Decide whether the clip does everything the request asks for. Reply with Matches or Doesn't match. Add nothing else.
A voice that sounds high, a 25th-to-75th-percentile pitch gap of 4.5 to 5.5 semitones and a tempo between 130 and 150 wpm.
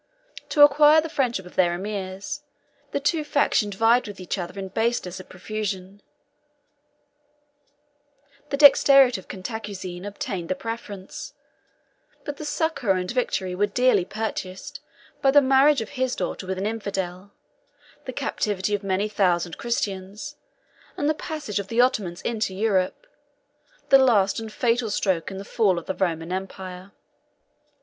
Matches